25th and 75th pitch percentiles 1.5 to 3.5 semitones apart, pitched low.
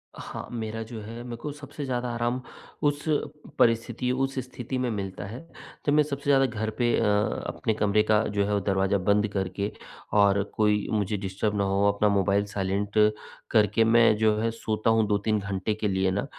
Yes: average, 2.8 semitones; low, 110 Hz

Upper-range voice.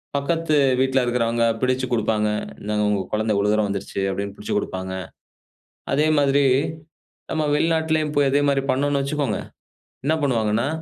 No: low, 130 Hz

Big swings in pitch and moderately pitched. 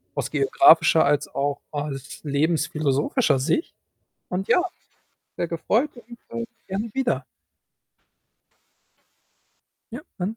Yes: wide, 7.3 semitones; medium, 160 Hz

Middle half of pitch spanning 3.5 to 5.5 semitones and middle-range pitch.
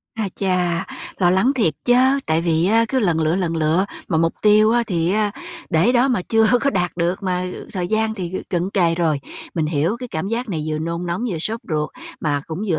Yes: average, 4.8 semitones; medium, 180 Hz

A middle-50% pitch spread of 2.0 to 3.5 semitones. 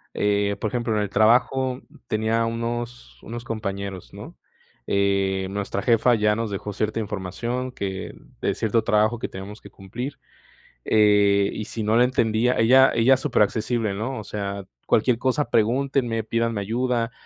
Yes: average, 2.9 semitones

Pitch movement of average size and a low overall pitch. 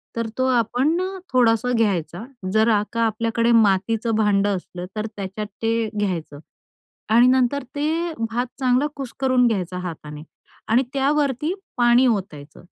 No: average, 3.9 semitones; high, 230 Hz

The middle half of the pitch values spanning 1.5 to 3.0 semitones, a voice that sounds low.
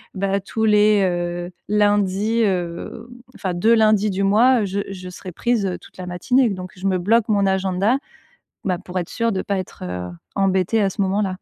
No: narrow, 2.4 semitones; high, 195 Hz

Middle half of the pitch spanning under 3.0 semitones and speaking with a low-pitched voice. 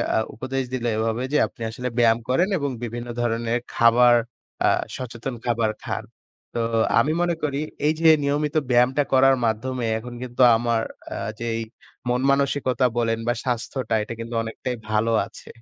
Yes: narrow, 2.4 semitones; low, 120 Hz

